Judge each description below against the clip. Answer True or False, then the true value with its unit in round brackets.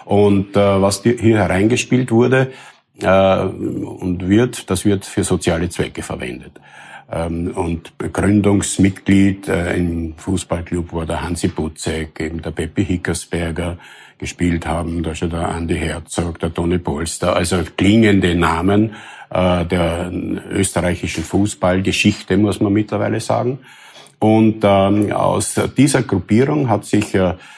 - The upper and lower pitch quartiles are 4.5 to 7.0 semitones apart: False (3.3 semitones)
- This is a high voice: False (95 Hz)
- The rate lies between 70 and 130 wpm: True (125 wpm)